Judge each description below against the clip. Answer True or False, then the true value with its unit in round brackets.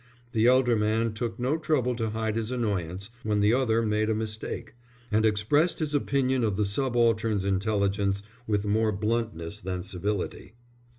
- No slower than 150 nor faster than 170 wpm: True (160 wpm)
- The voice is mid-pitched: False (110 Hz)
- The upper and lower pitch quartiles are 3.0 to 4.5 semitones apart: False (2.5 semitones)